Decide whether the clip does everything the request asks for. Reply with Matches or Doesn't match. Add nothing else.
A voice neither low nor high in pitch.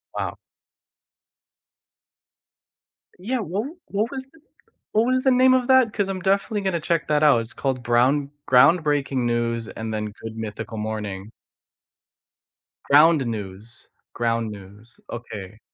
Doesn't match